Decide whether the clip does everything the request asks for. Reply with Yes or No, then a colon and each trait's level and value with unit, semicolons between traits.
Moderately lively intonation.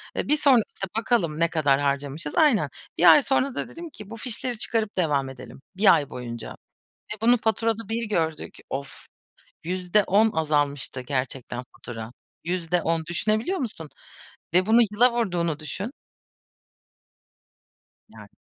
No: wide, 7.5 semitones